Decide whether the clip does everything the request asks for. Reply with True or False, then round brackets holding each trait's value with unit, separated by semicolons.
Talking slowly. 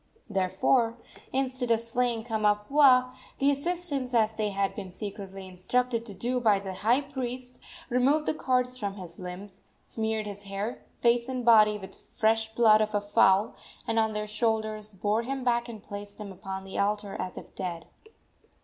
False (175 wpm)